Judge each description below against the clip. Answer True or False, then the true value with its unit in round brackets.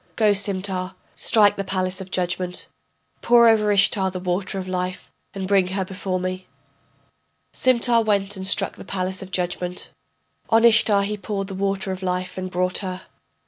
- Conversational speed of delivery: True (170 wpm)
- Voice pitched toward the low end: False (190 Hz)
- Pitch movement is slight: True (1.7 semitones)